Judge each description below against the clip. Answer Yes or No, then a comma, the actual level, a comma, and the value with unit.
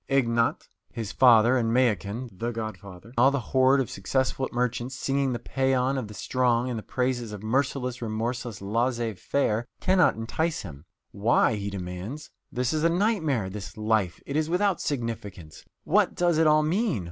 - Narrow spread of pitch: No, average, 4.0 semitones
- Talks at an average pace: Yes, average, 170 wpm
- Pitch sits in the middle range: No, low, 120 Hz